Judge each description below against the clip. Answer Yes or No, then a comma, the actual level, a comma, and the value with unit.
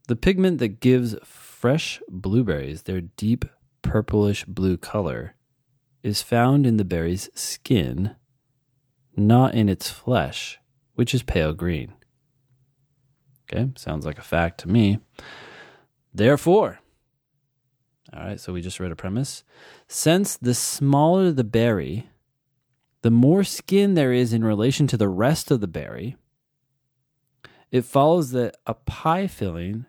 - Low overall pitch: Yes, low, 125 Hz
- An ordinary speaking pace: No, slow, 130 wpm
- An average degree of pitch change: Yes, average, 4.4 semitones